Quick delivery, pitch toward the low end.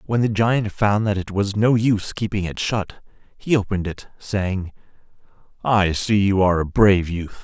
No: average, 185 wpm; low, 100 Hz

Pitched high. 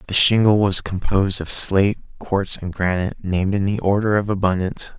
No: very low, 95 Hz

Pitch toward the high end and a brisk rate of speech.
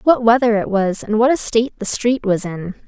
Yes: high, 225 Hz; fast, 250 wpm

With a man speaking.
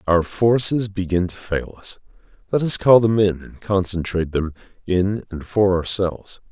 Yes: male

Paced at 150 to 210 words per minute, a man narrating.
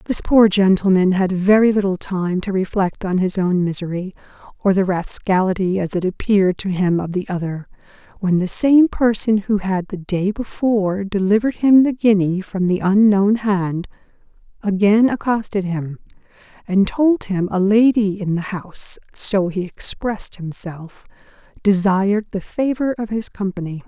No: average, 155 wpm; female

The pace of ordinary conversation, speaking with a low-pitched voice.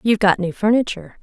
No: average, 195 wpm; high, 200 Hz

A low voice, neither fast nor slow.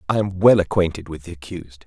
No: very low, 90 Hz; fast, 225 wpm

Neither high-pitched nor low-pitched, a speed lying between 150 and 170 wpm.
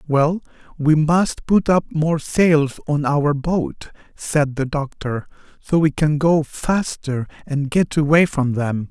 Yes: medium, 150 Hz; average, 155 wpm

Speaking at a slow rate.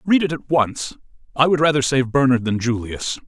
No: average, 200 wpm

